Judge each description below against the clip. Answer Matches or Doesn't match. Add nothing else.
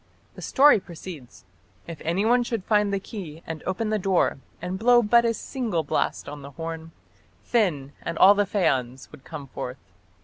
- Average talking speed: Matches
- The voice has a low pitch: Doesn't match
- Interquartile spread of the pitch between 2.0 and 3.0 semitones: Doesn't match